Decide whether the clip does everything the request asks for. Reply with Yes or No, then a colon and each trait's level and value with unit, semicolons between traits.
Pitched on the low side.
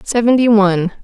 No: high, 215 Hz